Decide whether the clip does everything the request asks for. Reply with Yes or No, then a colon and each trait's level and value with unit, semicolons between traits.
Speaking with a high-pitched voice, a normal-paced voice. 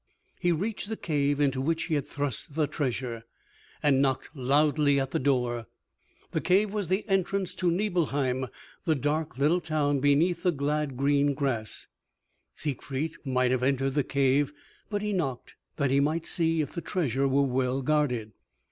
No: medium, 145 Hz; average, 165 wpm